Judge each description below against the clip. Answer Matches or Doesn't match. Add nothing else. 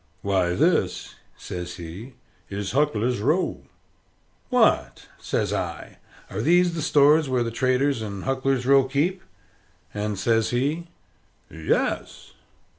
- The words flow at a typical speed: Doesn't match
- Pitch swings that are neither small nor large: Doesn't match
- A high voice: Doesn't match